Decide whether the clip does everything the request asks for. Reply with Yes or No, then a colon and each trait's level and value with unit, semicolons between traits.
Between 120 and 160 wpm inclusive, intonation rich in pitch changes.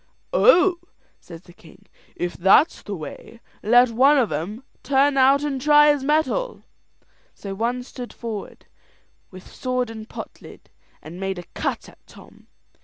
Yes: average, 155 wpm; wide, 6.5 semitones